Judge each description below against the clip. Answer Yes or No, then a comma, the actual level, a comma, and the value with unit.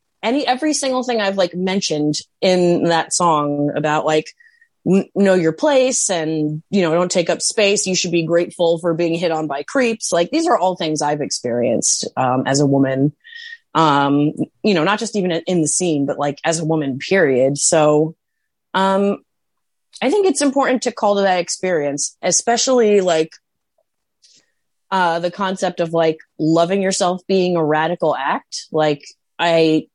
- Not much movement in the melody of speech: No, average, 4.2 semitones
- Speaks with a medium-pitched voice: Yes, medium, 175 Hz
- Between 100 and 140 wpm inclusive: No, average, 170 wpm